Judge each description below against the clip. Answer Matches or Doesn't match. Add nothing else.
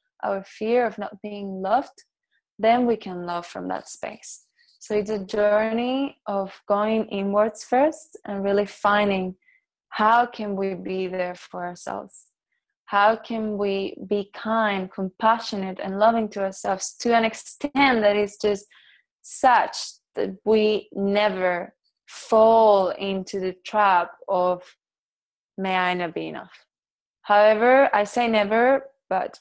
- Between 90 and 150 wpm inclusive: Matches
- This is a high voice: Matches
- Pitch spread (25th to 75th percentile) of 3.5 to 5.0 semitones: Doesn't match